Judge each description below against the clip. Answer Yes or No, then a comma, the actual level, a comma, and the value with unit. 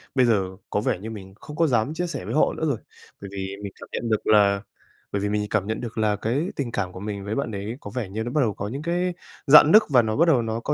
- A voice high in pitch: No, low, 110 Hz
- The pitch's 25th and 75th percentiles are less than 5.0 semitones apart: No, wide, 5.4 semitones